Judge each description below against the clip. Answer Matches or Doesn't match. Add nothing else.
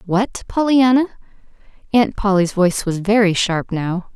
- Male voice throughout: Doesn't match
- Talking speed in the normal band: Doesn't match